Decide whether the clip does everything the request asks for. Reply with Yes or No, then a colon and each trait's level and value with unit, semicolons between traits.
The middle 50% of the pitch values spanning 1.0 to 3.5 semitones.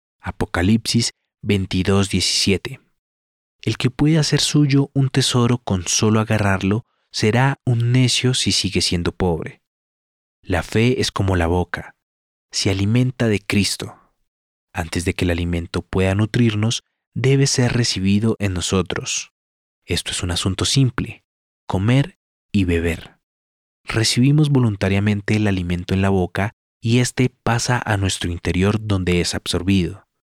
No: average, 5.2 semitones